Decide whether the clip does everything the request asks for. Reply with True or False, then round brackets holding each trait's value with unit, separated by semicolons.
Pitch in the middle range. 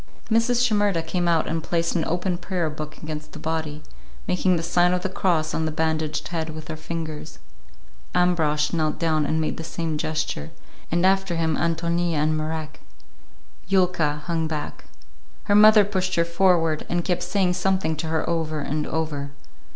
True (165 Hz)